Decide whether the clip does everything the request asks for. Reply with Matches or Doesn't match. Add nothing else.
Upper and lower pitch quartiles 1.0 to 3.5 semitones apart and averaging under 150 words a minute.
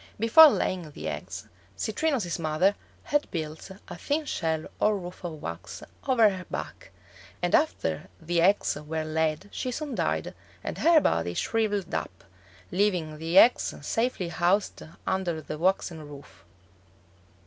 Doesn't match